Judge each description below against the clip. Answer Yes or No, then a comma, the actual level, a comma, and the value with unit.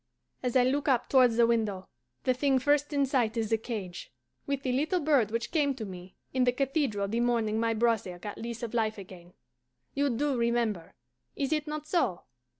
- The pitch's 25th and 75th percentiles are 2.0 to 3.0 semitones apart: No, average, 4.1 semitones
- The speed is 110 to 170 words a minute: No, average, 200 wpm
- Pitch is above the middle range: Yes, high, 240 Hz